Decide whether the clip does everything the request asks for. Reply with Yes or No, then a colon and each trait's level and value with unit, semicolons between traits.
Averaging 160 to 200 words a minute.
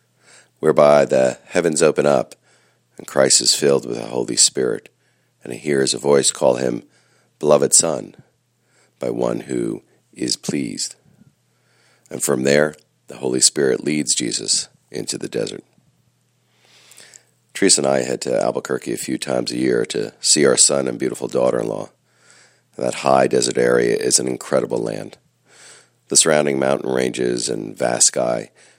No: average, 150 wpm